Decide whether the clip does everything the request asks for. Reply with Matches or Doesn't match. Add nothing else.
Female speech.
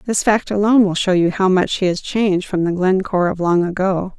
Matches